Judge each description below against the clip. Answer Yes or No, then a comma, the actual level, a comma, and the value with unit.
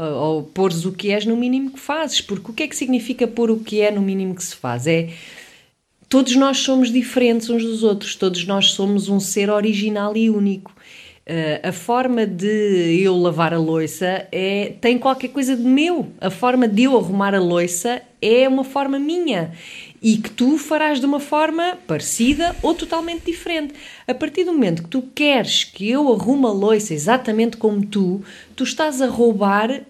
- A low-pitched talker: No, high, 230 Hz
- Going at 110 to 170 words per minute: No, average, 190 wpm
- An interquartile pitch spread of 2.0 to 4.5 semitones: No, wide, 5.4 semitones